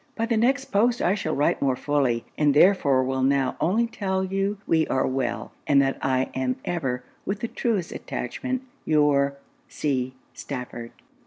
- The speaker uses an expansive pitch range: Yes, wide, 7.2 semitones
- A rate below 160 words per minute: No, average, 165 wpm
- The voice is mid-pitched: Yes, medium, 145 Hz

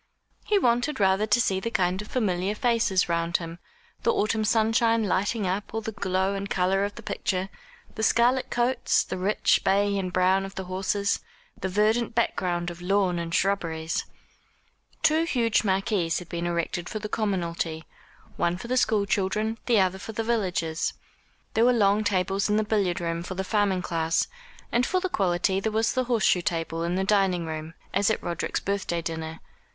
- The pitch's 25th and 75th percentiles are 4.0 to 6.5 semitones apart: No, average, 3.6 semitones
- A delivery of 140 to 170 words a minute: No, average, 185 wpm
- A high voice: Yes, high, 195 Hz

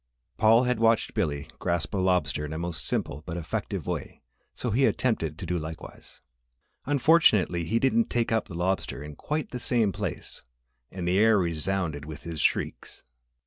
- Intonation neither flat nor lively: No, wide, 5.9 semitones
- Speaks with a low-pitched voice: Yes, very low, 95 Hz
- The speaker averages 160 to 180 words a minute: Yes, average, 175 wpm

